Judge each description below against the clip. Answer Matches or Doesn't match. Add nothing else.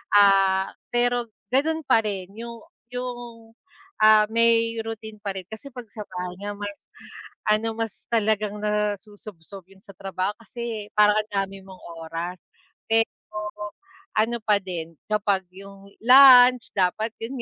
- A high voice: Matches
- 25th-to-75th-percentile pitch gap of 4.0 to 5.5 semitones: Doesn't match